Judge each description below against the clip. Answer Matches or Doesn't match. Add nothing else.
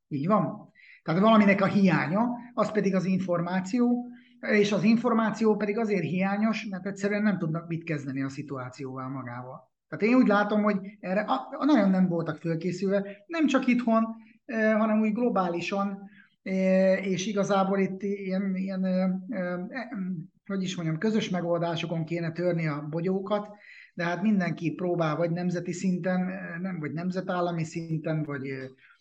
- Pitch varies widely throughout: Doesn't match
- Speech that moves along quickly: Doesn't match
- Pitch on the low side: Doesn't match